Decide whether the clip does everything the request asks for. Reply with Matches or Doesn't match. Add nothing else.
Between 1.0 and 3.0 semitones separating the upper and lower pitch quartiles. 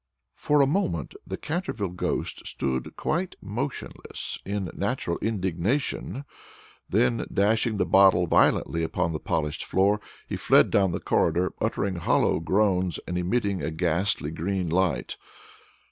Doesn't match